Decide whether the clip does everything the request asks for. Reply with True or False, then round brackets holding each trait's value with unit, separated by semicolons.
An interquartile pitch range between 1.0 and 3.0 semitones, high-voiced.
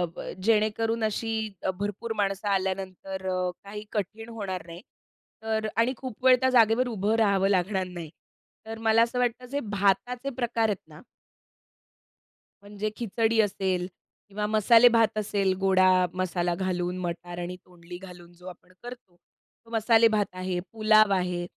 False (3.4 semitones; 205 Hz)